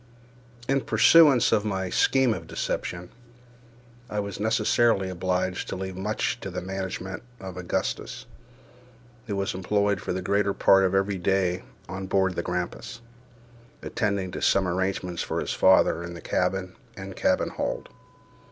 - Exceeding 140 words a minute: Yes, average, 150 wpm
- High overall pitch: No, very low, 95 Hz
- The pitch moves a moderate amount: No, narrow, 1.9 semitones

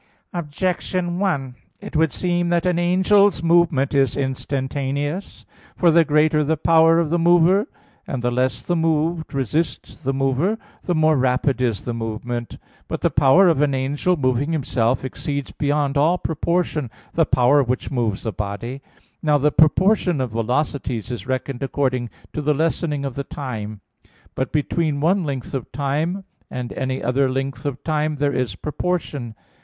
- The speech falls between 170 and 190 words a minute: No, average, 160 wpm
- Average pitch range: Yes, average, 4.2 semitones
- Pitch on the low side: No, medium, 145 Hz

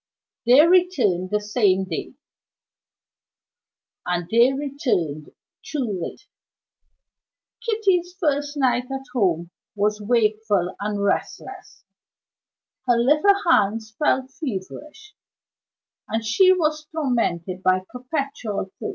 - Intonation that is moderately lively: No, wide, 6.8 semitones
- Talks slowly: Yes, slow, 100 wpm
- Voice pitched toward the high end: Yes, high, 245 Hz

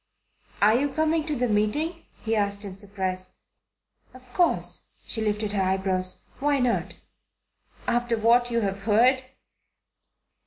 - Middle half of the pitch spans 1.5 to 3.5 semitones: No, average, 4.2 semitones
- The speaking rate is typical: No, slow, 130 wpm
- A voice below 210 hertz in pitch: No, high, 225 Hz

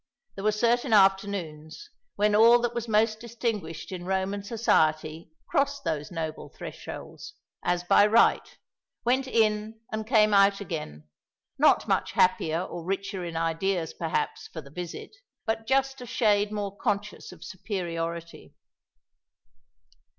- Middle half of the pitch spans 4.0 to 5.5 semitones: Yes, average, 4.8 semitones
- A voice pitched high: Yes, high, 200 Hz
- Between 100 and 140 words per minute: Yes, slow, 135 wpm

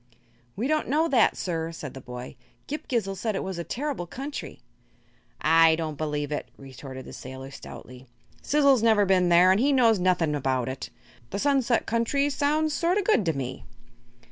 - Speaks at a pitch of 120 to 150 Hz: No, medium, 185 Hz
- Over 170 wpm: Yes, average, 180 wpm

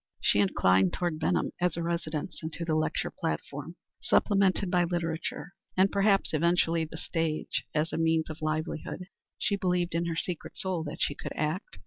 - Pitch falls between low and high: Yes, medium, 165 Hz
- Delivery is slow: No, average, 175 wpm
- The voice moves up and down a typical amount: No, narrow, 2.3 semitones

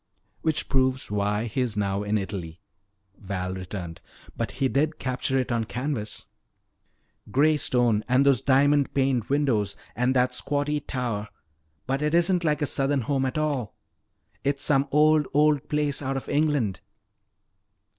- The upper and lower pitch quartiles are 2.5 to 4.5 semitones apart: No, average, 5.2 semitones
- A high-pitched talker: No, low, 130 Hz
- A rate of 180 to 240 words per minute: No, average, 150 wpm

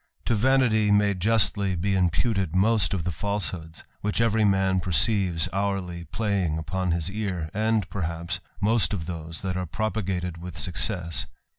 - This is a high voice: No, very low, 95 Hz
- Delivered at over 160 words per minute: No, average, 150 wpm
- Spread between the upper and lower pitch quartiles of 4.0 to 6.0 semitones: No, average, 3.3 semitones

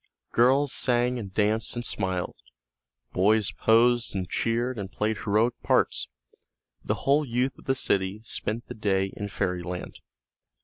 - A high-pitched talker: No, low, 110 Hz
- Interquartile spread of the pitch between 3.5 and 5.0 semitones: Yes, average, 3.8 semitones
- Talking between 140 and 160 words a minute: Yes, average, 145 wpm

